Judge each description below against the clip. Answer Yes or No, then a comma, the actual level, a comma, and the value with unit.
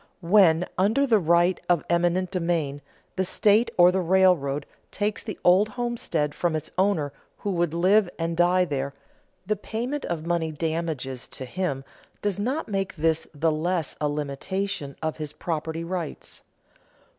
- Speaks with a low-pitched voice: No, medium, 175 Hz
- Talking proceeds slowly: No, average, 155 wpm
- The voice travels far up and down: No, average, 3.7 semitones